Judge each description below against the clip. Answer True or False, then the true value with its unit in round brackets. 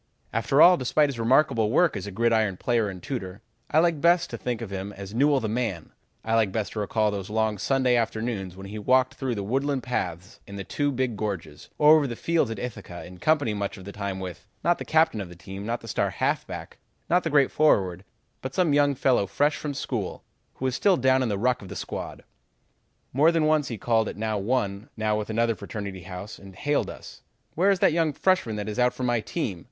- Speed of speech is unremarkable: False (230 wpm)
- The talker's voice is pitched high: False (115 Hz)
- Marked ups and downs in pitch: True (5.8 semitones)